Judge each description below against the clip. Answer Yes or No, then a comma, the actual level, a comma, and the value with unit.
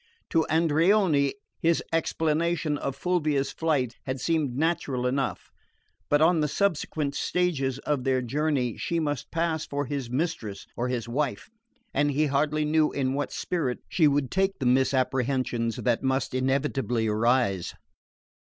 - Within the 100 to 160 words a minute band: Yes, average, 140 wpm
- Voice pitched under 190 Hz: Yes, medium, 140 Hz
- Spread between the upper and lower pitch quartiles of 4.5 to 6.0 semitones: No, average, 3.6 semitones